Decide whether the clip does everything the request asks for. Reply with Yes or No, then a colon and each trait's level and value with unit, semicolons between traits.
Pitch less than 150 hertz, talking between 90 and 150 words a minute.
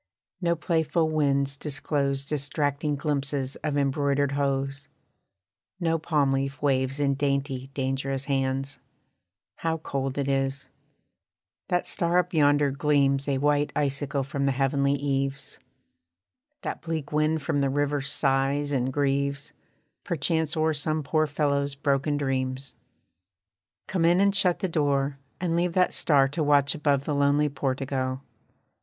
Yes: medium, 140 Hz; slow, 135 wpm